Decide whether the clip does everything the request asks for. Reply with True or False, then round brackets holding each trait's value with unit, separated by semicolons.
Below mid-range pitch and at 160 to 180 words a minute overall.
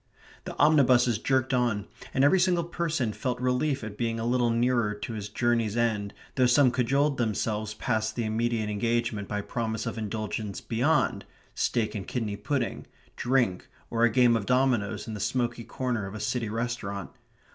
True (120 Hz; 170 wpm)